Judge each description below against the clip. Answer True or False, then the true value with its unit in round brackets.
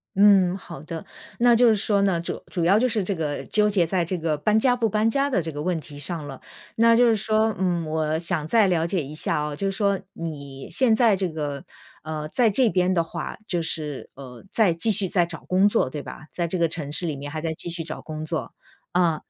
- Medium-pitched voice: True (175 Hz)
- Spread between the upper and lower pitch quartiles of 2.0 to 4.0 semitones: False (4.8 semitones)